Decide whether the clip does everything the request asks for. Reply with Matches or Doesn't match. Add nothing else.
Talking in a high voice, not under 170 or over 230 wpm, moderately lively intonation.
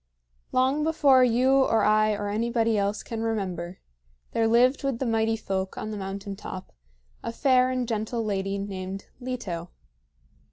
Doesn't match